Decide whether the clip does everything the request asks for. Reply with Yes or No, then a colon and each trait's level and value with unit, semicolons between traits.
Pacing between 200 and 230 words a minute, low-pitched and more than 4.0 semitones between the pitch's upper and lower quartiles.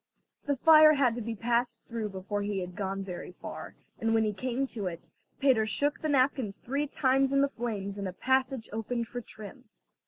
No: fast, 205 wpm; high, 235 Hz; average, 4.5 semitones